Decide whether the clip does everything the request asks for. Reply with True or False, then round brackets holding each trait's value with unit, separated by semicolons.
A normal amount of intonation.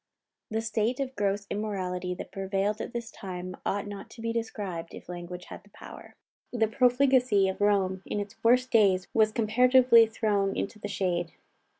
True (3.1 semitones)